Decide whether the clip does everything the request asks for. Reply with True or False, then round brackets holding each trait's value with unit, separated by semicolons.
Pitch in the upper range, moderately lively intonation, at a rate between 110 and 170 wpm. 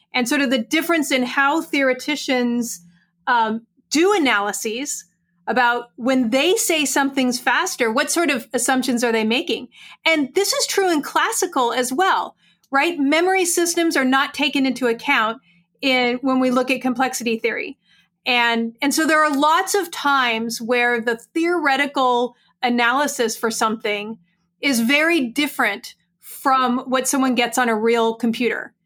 True (260 Hz; 3.8 semitones; 150 wpm)